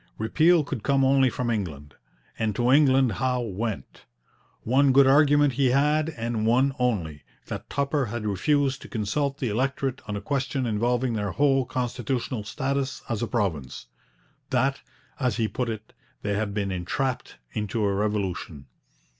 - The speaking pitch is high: No, low, 125 Hz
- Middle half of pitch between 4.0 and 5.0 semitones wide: Yes, average, 4.4 semitones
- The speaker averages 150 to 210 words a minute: Yes, average, 155 wpm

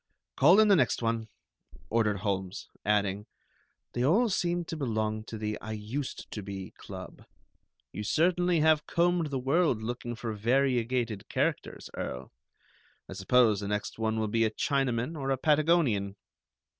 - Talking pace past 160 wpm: No, average, 155 wpm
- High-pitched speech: No, low, 115 Hz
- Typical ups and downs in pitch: No, wide, 6.0 semitones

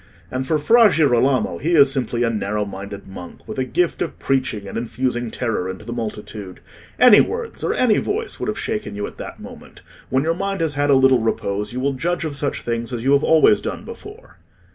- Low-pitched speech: Yes, low, 130 Hz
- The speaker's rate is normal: No, fast, 220 wpm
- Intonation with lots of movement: Yes, wide, 6.3 semitones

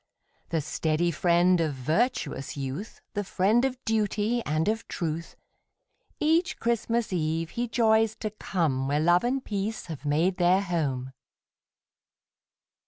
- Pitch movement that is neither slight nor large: No, wide, 6.0 semitones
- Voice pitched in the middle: Yes, medium, 180 Hz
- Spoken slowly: Yes, slow, 130 wpm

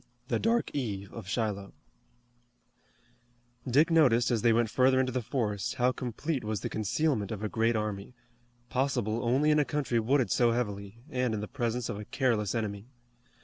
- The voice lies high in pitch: No, low, 115 Hz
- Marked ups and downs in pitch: No, average, 3.4 semitones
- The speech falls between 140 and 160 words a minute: No, average, 175 wpm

